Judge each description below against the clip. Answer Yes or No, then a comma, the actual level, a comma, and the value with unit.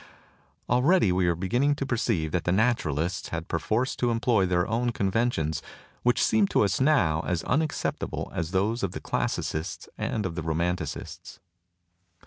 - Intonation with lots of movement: Yes, wide, 6.3 semitones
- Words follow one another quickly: No, average, 160 wpm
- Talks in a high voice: No, very low, 95 Hz